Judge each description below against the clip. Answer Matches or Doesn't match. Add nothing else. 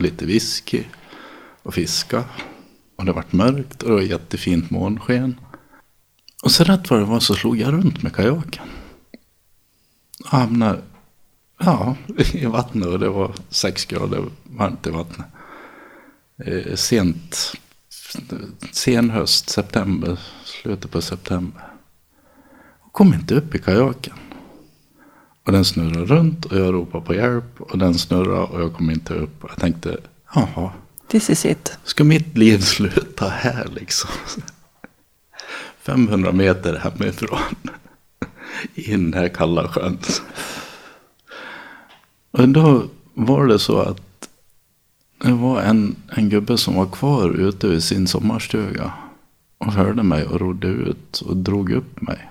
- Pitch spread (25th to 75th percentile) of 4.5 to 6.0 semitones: Matches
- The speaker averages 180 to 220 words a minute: Doesn't match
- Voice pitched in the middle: Doesn't match